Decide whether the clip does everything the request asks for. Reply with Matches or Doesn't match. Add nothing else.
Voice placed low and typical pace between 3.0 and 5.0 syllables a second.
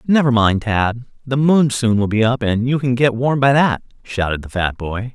Matches